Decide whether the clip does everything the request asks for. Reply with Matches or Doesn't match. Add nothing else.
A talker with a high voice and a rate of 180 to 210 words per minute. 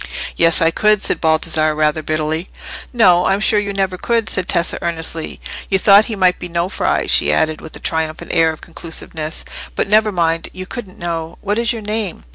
Doesn't match